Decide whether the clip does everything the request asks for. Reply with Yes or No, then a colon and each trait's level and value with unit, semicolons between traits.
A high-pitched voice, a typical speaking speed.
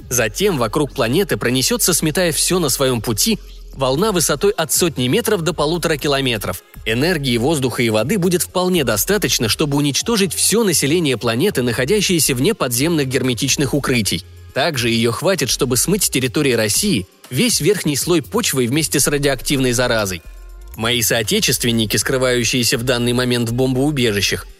No: low, 135 Hz; average, 140 wpm